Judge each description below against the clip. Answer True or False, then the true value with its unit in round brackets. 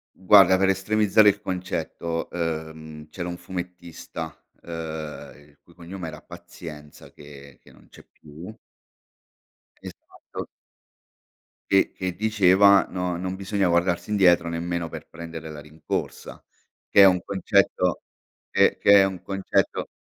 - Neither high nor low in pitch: False (90 Hz)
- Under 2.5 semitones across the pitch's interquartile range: False (2.9 semitones)